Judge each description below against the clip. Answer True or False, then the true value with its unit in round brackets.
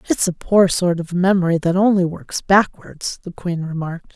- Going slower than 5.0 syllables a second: True (4.8 syllables/s)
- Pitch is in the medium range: True (180 Hz)